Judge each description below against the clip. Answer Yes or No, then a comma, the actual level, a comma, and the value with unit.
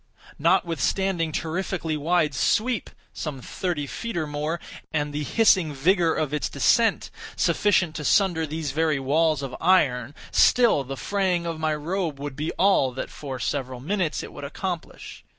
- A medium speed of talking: Yes, average, 160 wpm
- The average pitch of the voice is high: No, medium, 160 Hz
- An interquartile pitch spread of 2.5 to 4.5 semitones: Yes, average, 3.9 semitones